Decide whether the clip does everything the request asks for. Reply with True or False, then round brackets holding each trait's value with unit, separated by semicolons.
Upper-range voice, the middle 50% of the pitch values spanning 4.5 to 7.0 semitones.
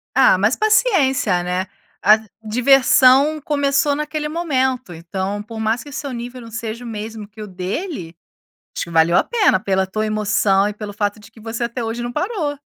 True (230 Hz; 5.3 semitones)